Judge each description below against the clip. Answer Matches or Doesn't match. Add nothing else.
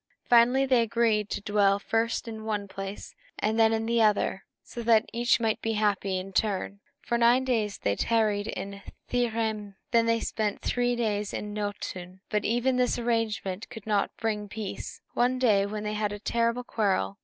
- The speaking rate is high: Doesn't match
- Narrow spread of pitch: Matches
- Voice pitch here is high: Matches